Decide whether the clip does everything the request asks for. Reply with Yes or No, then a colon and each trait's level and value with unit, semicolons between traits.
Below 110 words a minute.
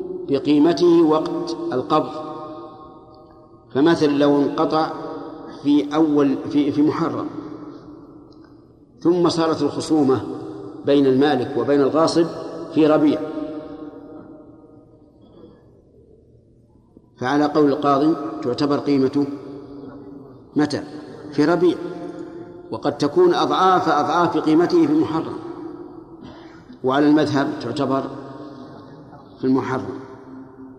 Yes: average, 80 wpm